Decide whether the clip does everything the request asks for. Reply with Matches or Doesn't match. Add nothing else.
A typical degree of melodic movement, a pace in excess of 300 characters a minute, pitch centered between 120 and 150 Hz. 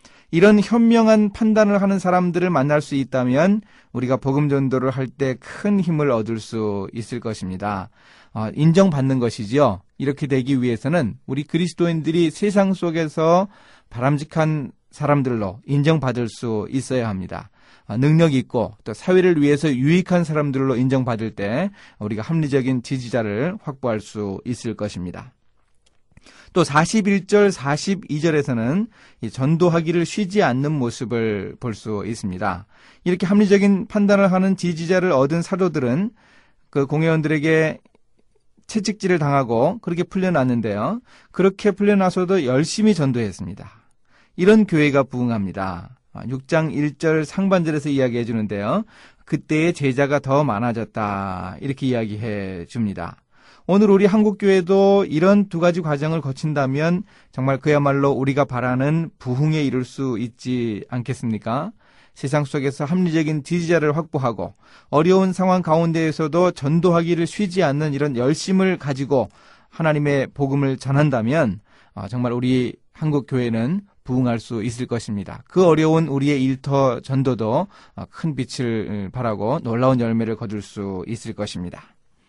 Doesn't match